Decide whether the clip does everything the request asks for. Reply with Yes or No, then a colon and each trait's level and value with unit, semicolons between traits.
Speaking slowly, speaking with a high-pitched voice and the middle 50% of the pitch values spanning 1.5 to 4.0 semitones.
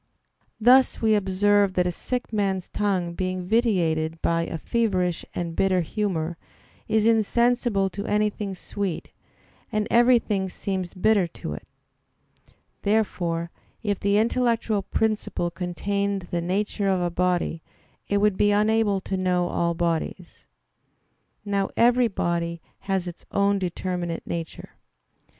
Yes: slow, 130 wpm; high, 195 Hz; average, 3.2 semitones